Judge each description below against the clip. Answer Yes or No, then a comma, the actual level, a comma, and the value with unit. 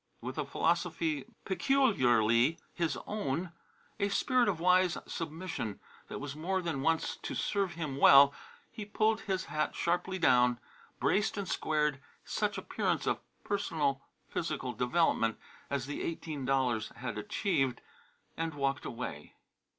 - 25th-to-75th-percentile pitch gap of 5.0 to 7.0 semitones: Yes, wide, 5.5 semitones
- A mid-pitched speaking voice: Yes, medium, 160 Hz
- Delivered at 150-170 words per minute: No, slow, 135 wpm